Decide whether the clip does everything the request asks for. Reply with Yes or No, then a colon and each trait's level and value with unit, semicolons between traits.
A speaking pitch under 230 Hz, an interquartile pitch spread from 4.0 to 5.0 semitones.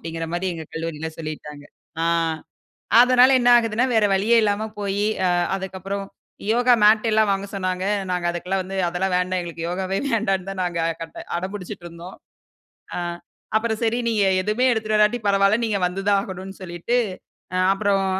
No: high, 195 Hz; average, 3.2 semitones